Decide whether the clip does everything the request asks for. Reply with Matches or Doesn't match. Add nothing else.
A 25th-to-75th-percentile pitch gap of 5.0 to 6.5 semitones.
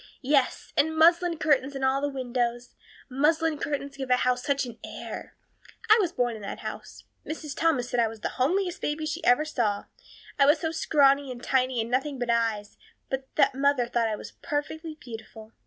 Doesn't match